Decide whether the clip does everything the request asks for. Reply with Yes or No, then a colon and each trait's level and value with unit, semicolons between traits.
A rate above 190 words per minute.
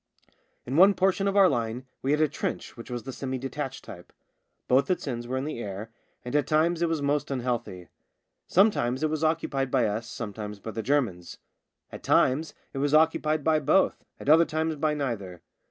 Yes: average, 200 wpm